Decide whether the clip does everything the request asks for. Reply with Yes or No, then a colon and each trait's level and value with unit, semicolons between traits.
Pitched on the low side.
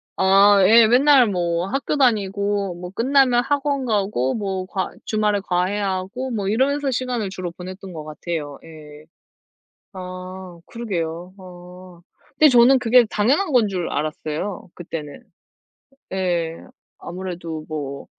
No: high, 190 Hz